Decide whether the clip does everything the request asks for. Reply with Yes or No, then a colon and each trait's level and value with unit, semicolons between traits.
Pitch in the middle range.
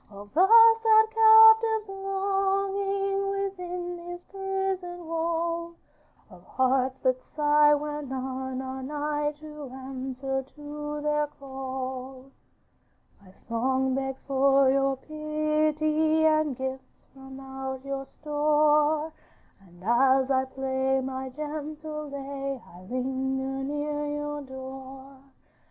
No: very high, 290 Hz